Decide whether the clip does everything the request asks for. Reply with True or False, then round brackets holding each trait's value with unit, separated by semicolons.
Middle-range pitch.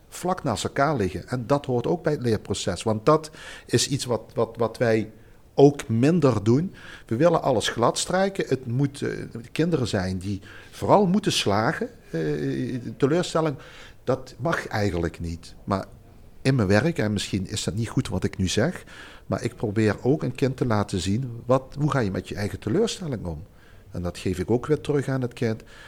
False (120 Hz)